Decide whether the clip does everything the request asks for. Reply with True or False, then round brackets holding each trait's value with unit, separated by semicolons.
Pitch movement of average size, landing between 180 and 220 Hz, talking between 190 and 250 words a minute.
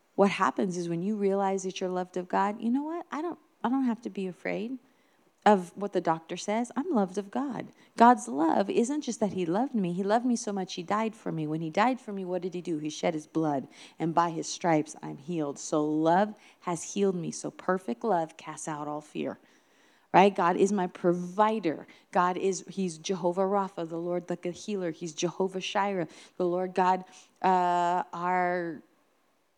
True (3.1 semitones; 185 Hz; 205 wpm)